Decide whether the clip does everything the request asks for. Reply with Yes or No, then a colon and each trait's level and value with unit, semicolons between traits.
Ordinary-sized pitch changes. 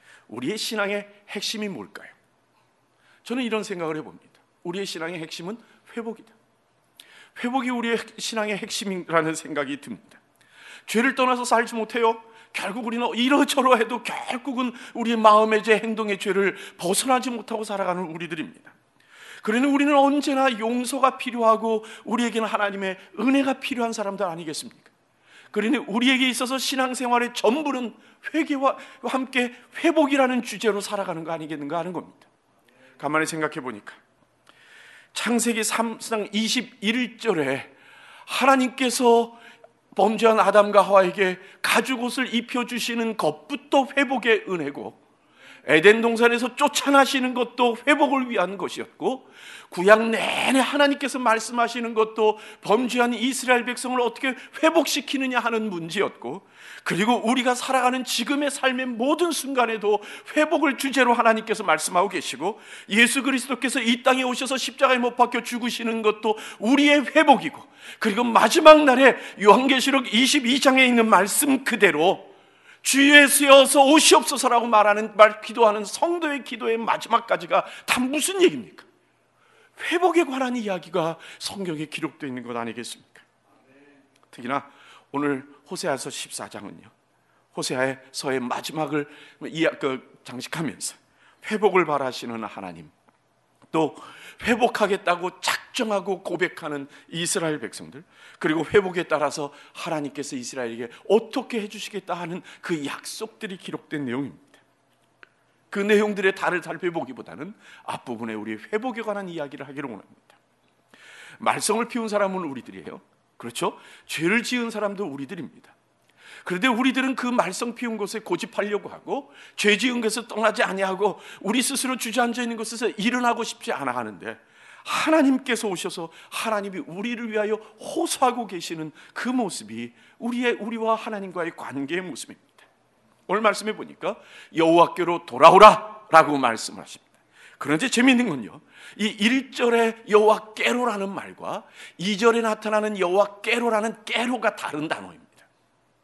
Yes: average, 4.8 semitones